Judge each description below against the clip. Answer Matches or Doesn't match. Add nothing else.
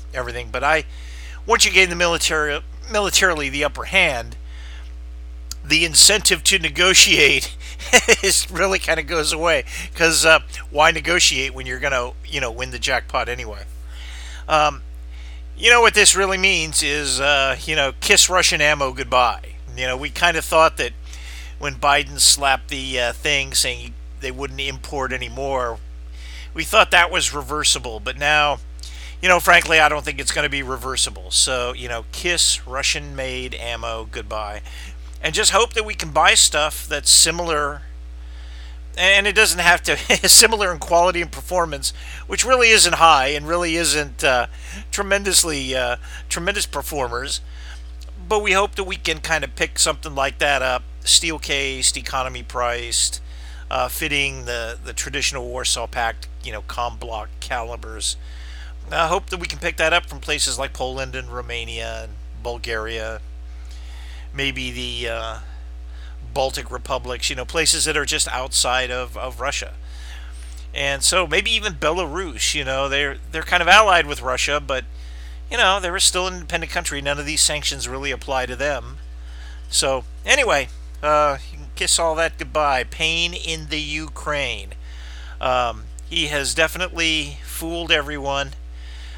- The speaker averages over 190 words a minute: Doesn't match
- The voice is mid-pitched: Doesn't match